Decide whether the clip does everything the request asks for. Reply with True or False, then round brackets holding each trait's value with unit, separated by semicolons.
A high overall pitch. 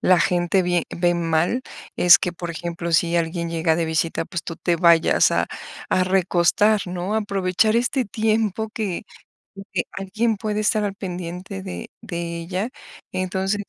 False (180 Hz)